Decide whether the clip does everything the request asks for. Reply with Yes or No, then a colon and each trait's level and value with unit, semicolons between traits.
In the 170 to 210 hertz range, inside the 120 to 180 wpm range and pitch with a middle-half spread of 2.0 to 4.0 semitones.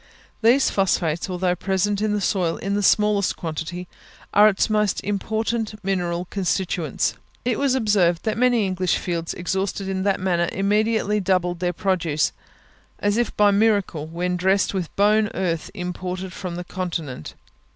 Yes: high, 190 Hz; average, 155 wpm; average, 2.8 semitones